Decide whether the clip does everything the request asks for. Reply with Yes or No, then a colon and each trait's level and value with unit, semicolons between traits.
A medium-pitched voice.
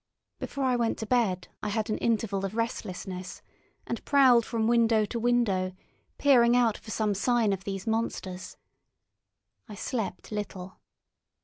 No: high, 220 Hz